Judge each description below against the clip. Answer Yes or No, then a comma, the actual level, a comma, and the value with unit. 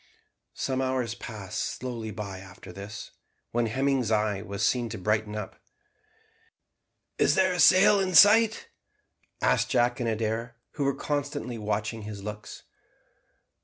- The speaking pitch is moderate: No, low, 115 Hz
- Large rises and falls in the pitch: No, average, 3.9 semitones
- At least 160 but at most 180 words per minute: No, slow, 135 wpm